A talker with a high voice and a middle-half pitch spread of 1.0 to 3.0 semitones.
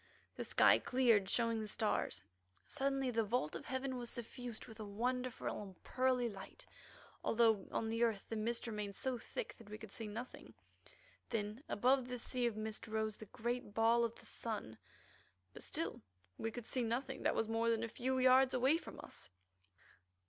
Yes: high, 230 Hz; narrow, 2.6 semitones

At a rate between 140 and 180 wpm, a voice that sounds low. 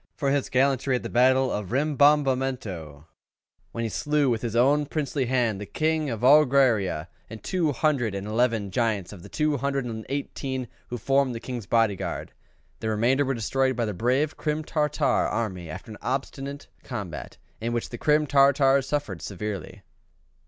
Yes: average, 175 wpm; low, 130 Hz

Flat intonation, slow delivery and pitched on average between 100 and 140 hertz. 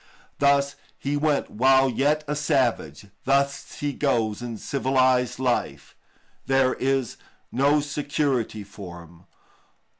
No: average, 3.0 semitones; slow, 115 wpm; low, 135 Hz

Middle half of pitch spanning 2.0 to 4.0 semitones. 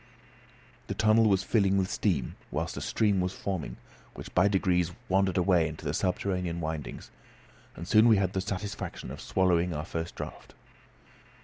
Yes: average, 2.7 semitones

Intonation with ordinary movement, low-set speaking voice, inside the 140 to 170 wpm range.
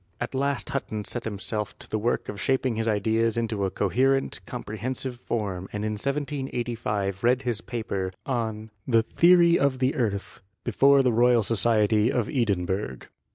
Yes: average, 3.6 semitones; low, 115 Hz; average, 160 wpm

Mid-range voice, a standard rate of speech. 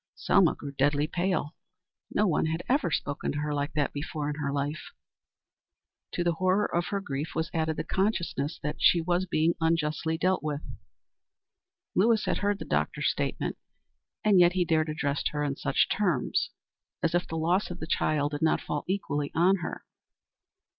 Yes: medium, 160 Hz; average, 180 wpm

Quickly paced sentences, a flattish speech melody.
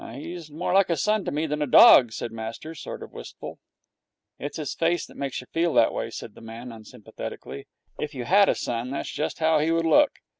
No: fast, 225 wpm; average, 5.1 semitones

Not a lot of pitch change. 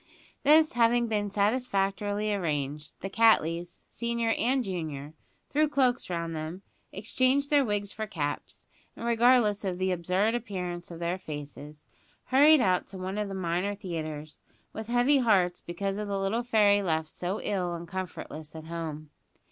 No: average, 5.1 semitones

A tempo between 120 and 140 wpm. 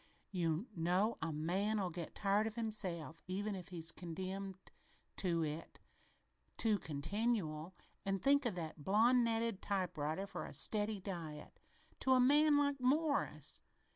Yes: slow, 135 wpm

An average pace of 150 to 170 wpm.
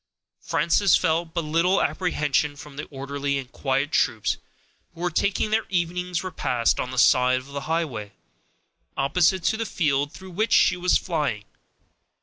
Yes: average, 155 wpm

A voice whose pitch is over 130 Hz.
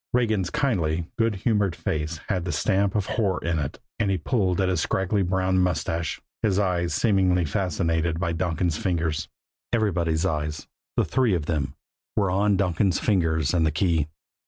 No: very low, 90 Hz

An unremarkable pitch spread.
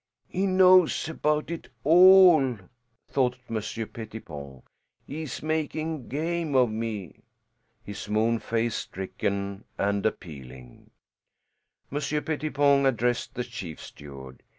No: wide, 7.4 semitones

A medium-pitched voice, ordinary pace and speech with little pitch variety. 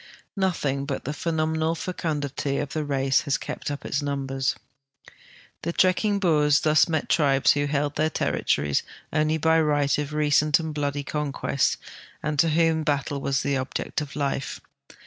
Yes: medium, 150 Hz; average, 165 wpm; narrow, 2.2 semitones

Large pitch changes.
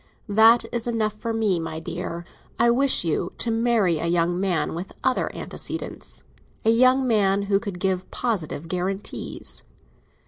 No: average, 4.5 semitones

